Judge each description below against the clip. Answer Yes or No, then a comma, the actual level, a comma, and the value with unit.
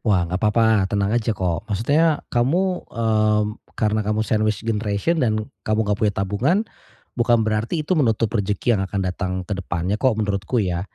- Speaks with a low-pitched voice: Yes, low, 110 Hz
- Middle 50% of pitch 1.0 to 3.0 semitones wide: Yes, average, 2.7 semitones